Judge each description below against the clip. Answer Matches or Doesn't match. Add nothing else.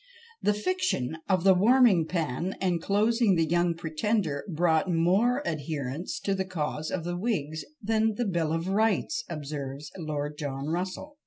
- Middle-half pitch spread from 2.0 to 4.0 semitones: Doesn't match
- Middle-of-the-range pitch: Matches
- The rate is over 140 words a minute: Matches